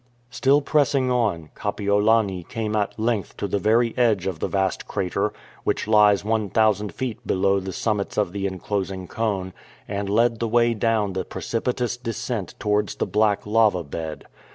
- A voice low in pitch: Yes, low, 105 Hz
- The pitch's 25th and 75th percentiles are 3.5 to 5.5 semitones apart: No, average, 2.8 semitones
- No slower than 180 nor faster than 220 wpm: No, average, 165 wpm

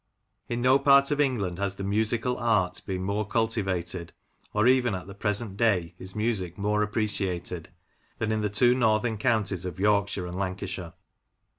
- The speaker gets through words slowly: No, average, 165 wpm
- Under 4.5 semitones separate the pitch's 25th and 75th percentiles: Yes, average, 3.5 semitones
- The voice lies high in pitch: No, low, 105 Hz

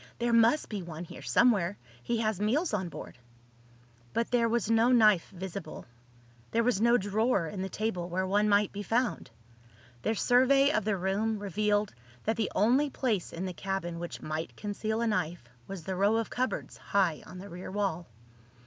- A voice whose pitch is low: No, high, 205 Hz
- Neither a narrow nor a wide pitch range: Yes, average, 3.5 semitones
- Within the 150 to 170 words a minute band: No, average, 185 wpm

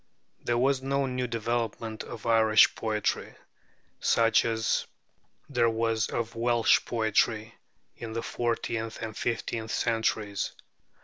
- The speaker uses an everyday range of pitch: No, narrow, 1.1 semitones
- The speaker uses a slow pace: Yes, slow, 115 wpm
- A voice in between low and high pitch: No, low, 115 Hz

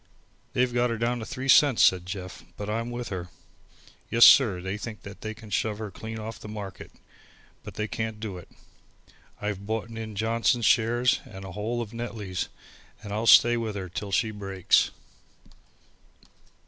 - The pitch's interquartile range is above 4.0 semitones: No, narrow, 2.6 semitones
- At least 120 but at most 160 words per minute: No, average, 175 wpm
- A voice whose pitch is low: Yes, low, 110 Hz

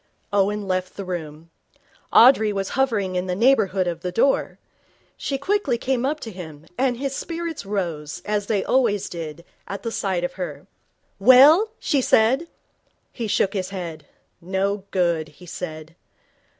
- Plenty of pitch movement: Yes, wide, 5.7 semitones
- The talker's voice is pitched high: Yes, high, 195 Hz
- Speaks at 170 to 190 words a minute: No, average, 155 wpm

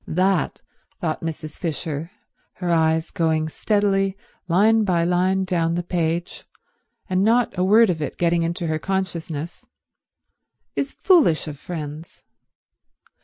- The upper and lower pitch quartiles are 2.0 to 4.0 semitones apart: Yes, average, 3.0 semitones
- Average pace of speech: No, slow, 130 wpm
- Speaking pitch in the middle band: Yes, medium, 175 Hz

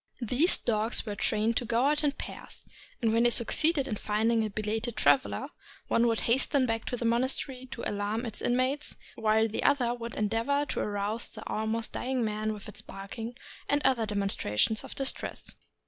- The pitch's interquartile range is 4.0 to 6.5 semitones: No, average, 2.9 semitones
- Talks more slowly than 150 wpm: No, average, 180 wpm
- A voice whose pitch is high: Yes, high, 230 Hz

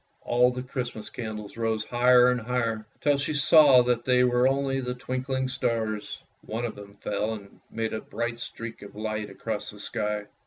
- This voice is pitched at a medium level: No, low, 120 Hz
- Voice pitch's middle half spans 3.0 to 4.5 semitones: No, narrow, 2.5 semitones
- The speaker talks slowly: No, average, 185 wpm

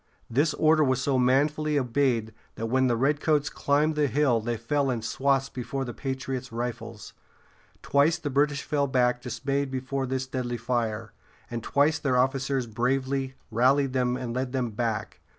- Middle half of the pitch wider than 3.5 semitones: No, narrow, 2.6 semitones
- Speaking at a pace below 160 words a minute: No, average, 170 wpm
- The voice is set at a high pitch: No, low, 130 Hz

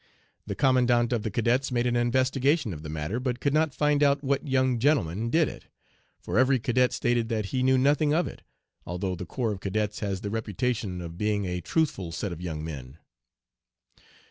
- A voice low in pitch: Yes, low, 120 Hz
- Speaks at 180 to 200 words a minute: Yes, average, 195 wpm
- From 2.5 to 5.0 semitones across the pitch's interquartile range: No, wide, 5.4 semitones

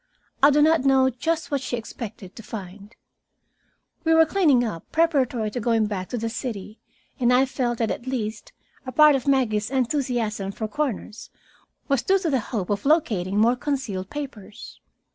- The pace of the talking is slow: No, average, 175 wpm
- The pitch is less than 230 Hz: No, high, 245 Hz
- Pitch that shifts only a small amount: No, average, 4.6 semitones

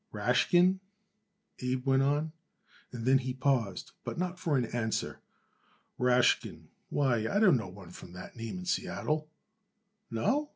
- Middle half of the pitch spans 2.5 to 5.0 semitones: No, wide, 5.5 semitones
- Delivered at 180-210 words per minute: No, average, 150 wpm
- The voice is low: Yes, low, 130 Hz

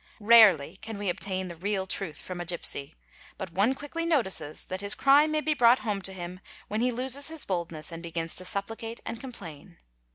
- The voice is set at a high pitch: Yes, high, 200 Hz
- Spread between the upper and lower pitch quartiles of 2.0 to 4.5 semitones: No, average, 5.2 semitones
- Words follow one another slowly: No, fast, 205 wpm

